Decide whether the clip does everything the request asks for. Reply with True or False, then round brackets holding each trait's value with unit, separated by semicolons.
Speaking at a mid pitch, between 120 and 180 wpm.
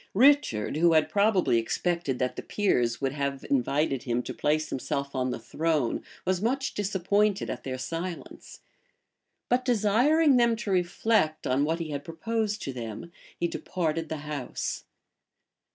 True (165 Hz; 150 wpm)